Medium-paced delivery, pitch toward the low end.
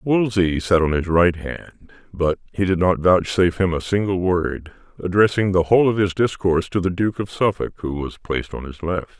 No: fast, 210 wpm; very low, 90 Hz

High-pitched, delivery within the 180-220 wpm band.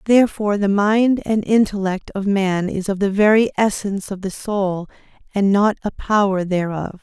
No: high, 200 Hz; average, 170 wpm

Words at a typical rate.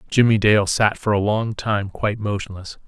Yes: average, 190 wpm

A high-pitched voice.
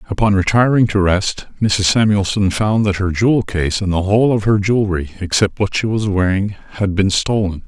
No: low, 100 Hz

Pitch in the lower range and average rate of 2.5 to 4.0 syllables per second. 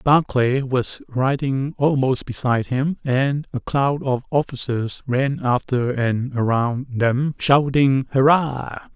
Yes: low, 130 Hz; 3.6 syllables/s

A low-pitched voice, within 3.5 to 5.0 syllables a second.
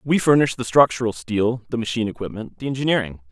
No: low, 115 Hz; 6.4 syllables/s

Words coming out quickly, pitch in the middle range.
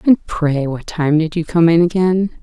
Yes: fast, 225 wpm; medium, 165 Hz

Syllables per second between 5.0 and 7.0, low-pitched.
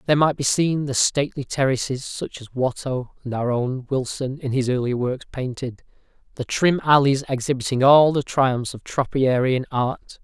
No: 4.8 syllables/s; low, 130 Hz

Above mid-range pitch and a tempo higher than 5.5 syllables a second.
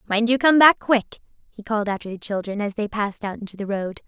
Yes: high, 215 Hz; 6.2 syllables/s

